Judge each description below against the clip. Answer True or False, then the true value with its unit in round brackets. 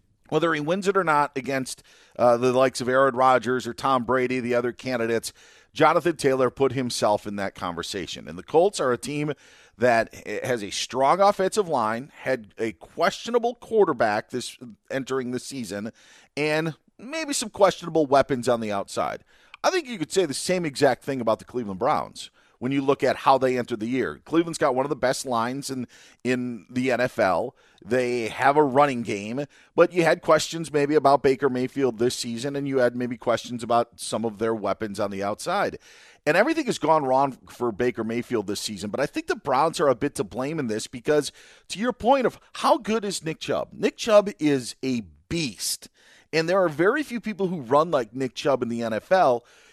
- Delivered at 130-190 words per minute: False (200 wpm)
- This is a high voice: False (135 Hz)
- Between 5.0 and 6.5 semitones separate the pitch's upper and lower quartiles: True (5.3 semitones)